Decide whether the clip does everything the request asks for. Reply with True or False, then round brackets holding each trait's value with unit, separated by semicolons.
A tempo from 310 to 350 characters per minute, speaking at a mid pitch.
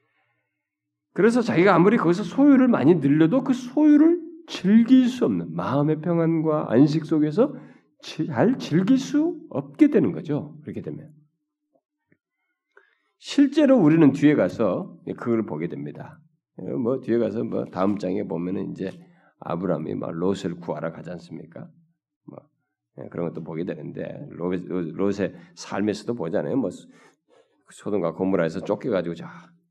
False (280 characters per minute; 155 Hz)